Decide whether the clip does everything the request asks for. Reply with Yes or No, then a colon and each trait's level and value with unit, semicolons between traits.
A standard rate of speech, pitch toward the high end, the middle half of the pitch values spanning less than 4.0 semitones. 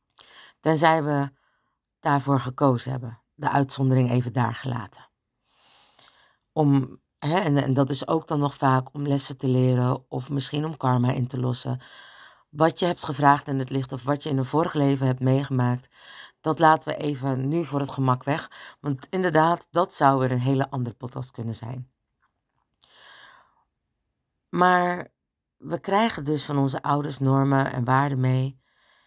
No: average, 160 wpm; low, 135 Hz; narrow, 2.4 semitones